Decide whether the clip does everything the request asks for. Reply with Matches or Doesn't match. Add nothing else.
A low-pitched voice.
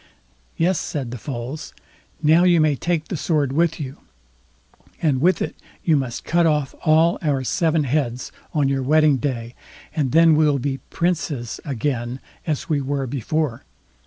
Doesn't match